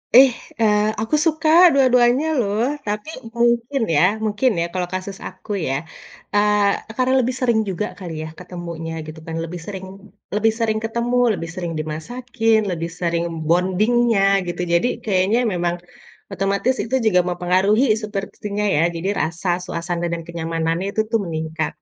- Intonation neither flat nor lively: Yes, average, 5.0 semitones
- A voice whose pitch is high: Yes, high, 200 Hz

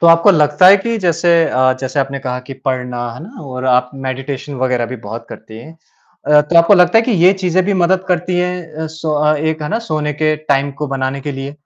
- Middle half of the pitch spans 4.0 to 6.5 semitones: Yes, average, 5.0 semitones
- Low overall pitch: No, medium, 150 Hz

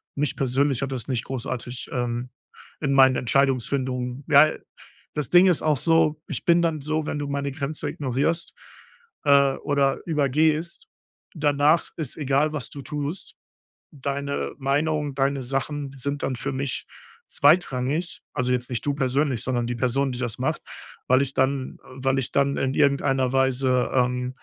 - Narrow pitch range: Yes, narrow, 2.2 semitones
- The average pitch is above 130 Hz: Yes, medium, 140 Hz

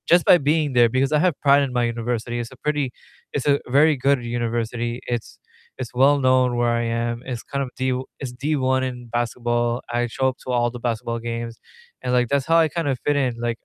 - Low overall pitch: Yes, low, 125 Hz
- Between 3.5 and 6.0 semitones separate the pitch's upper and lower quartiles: No, average, 2.7 semitones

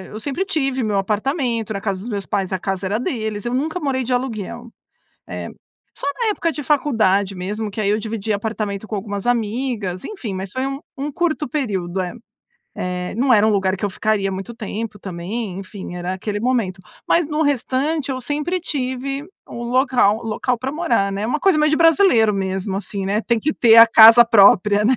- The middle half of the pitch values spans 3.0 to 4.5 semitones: No, average, 5.1 semitones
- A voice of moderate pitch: No, high, 225 Hz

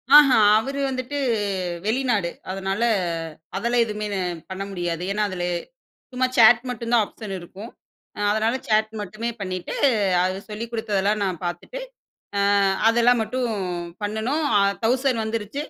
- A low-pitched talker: No, high, 220 Hz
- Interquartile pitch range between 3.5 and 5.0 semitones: Yes, average, 3.8 semitones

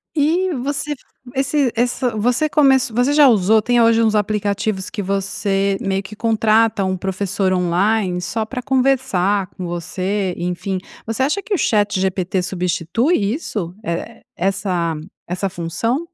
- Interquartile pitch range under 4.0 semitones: No, average, 4.7 semitones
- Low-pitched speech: No, high, 205 Hz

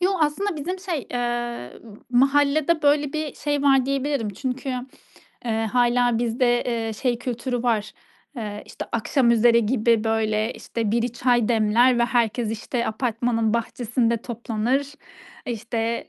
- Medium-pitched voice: No, high, 240 Hz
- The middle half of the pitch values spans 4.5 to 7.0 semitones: No, average, 3.0 semitones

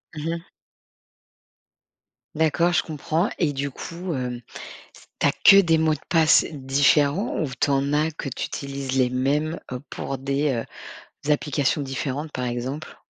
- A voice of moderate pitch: Yes, medium, 145 Hz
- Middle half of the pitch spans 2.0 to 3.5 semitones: Yes, average, 2.8 semitones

